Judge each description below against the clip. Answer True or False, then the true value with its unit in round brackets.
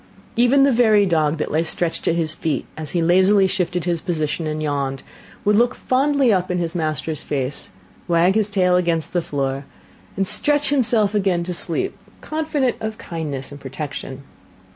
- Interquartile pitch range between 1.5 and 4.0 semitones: False (5.3 semitones)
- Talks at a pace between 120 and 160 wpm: False (175 wpm)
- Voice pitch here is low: False (175 Hz)